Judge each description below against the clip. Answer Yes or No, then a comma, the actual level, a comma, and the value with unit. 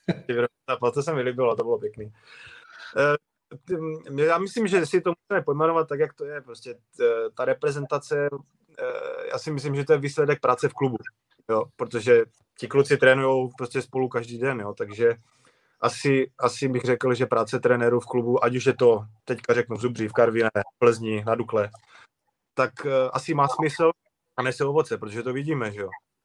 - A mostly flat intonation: No, wide, 5.5 semitones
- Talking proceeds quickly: Yes, fast, 175 wpm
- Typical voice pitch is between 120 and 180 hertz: Yes, low, 135 Hz